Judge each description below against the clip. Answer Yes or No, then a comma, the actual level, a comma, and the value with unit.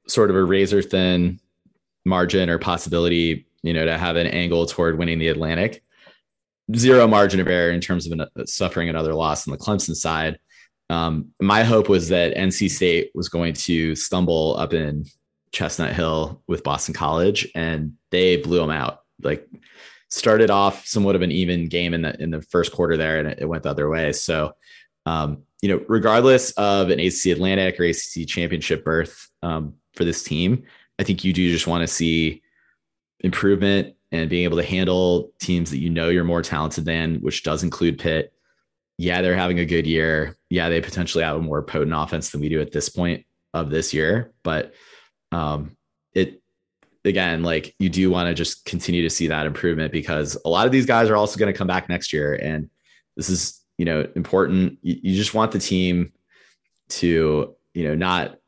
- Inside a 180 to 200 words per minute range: Yes, average, 195 wpm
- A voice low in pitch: Yes, very low, 85 Hz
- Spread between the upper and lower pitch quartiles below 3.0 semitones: Yes, narrow, 2.5 semitones